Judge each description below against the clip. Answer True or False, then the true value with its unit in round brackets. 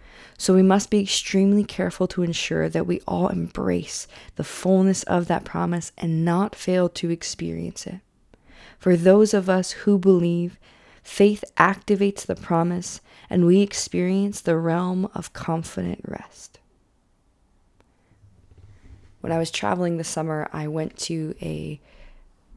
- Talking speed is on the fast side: False (135 wpm)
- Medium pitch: True (170 Hz)